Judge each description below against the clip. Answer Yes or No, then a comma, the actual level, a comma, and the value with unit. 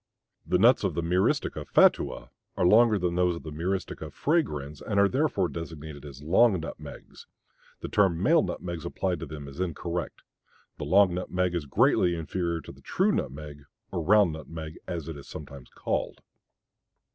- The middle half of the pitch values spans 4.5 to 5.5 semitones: No, average, 3.5 semitones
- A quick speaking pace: No, average, 160 wpm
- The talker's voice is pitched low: Yes, very low, 85 Hz